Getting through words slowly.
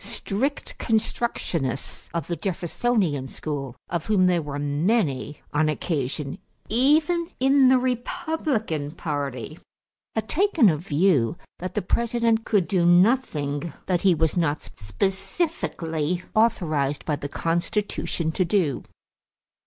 Yes: slow, 120 wpm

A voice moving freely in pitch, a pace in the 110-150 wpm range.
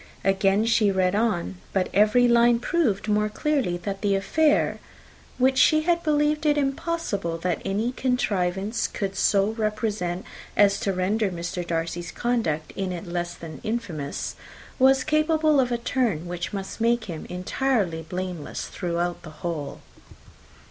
Yes: wide, 5.7 semitones; average, 145 wpm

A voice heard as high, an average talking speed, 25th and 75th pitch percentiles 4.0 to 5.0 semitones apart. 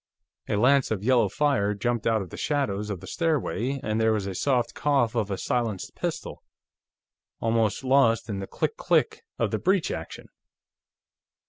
No: low, 115 Hz; average, 170 wpm; average, 4.5 semitones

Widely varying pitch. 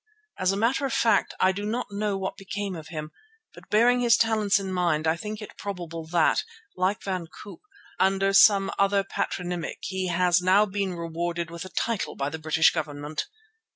No: average, 3.2 semitones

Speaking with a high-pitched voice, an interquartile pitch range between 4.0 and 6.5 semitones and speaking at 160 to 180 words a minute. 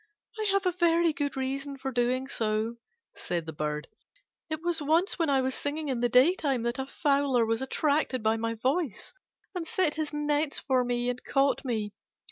No: very high, 270 Hz; average, 4.4 semitones; average, 190 wpm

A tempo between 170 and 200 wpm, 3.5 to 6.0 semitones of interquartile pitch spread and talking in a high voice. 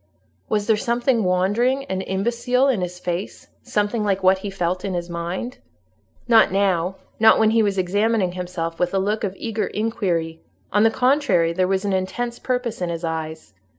Yes: average, 180 wpm; average, 3.9 semitones; high, 195 Hz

